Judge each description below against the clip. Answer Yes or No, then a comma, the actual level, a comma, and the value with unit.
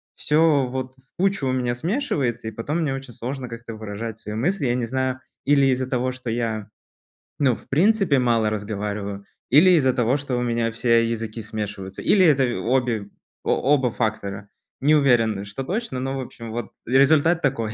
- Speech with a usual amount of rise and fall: Yes, average, 3.5 semitones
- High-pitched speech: No, low, 125 Hz